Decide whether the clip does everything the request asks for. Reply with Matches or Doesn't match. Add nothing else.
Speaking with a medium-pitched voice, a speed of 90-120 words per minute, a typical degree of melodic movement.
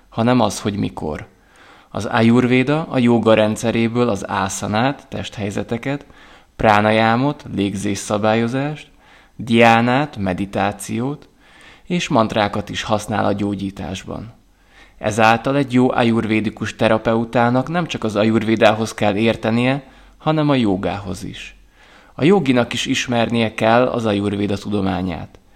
Doesn't match